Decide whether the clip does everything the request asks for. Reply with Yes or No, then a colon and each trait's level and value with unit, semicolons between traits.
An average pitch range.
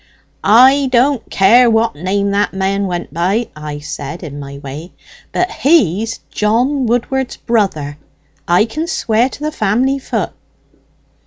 No: wide, 6.2 semitones